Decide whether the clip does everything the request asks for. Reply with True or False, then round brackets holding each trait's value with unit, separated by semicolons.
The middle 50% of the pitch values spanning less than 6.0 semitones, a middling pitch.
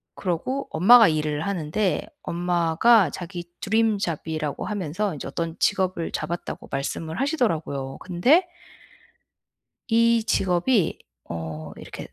True (5.5 semitones; 175 Hz)